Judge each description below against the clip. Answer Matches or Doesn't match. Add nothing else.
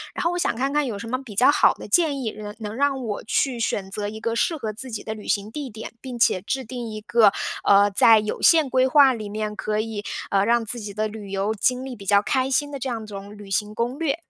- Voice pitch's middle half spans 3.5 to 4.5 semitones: Matches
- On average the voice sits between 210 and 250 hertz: Matches